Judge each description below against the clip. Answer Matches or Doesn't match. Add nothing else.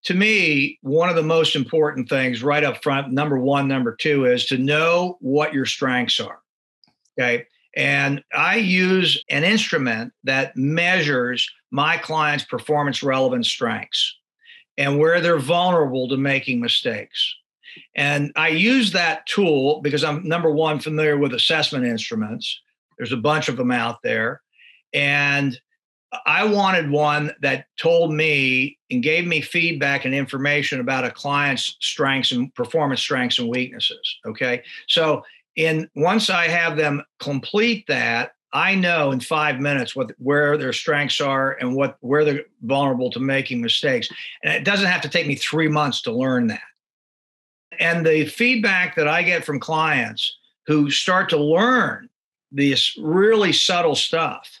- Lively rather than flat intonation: Doesn't match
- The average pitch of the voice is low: Doesn't match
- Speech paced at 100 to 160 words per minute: Matches